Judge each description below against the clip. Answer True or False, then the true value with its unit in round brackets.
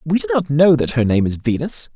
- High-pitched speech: False (135 Hz)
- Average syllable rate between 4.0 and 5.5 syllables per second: False (5.7 syllables/s)